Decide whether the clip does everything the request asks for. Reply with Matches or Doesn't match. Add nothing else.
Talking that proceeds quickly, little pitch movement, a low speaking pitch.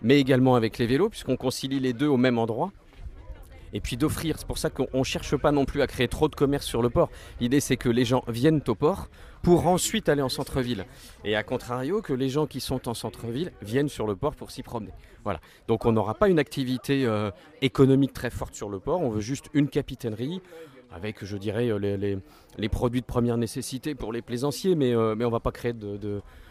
Doesn't match